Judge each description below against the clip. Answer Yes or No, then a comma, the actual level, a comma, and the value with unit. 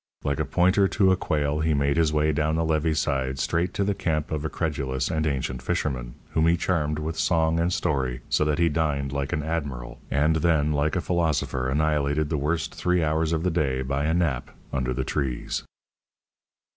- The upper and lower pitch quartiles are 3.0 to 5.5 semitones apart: No, narrow, 2.6 semitones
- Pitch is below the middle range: Yes, very low, 75 Hz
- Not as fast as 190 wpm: No, fast, 205 wpm